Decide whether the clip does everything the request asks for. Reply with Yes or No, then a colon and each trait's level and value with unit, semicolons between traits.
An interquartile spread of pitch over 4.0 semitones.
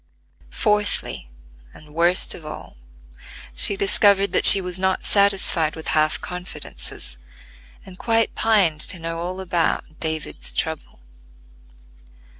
No: average, 3.7 semitones